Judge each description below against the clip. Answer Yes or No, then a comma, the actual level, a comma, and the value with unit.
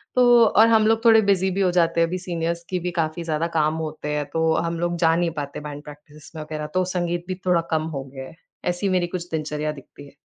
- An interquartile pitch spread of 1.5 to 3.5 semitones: Yes, average, 2.8 semitones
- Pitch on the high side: No, medium, 170 Hz